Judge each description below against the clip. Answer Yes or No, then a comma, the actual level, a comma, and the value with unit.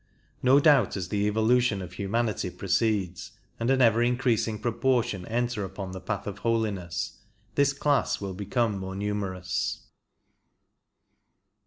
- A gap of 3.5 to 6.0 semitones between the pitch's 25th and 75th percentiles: Yes, average, 3.9 semitones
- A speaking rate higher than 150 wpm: No, average, 140 wpm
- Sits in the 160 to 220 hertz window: No, low, 105 Hz